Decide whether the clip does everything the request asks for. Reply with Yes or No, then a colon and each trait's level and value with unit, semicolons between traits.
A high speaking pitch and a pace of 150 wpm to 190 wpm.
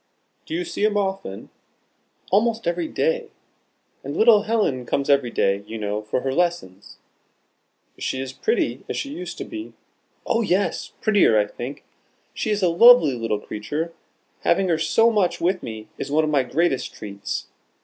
No: medium, 170 Hz; average, 170 wpm